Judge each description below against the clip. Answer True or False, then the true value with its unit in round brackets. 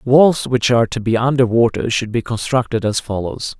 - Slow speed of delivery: False (200 wpm)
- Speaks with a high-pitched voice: False (120 Hz)